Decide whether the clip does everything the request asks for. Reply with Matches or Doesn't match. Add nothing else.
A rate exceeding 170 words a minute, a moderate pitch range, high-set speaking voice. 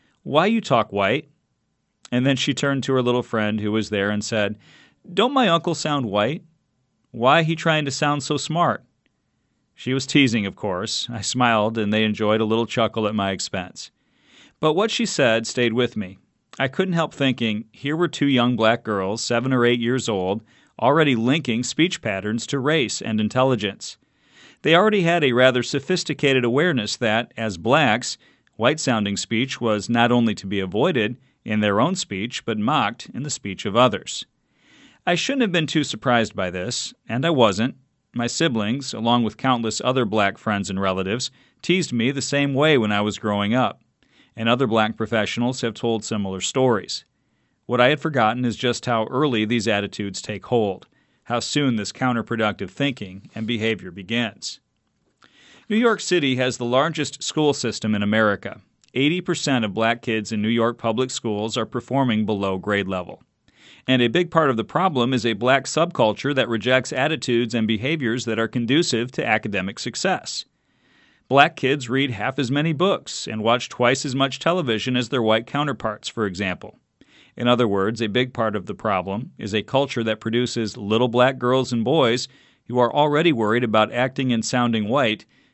Doesn't match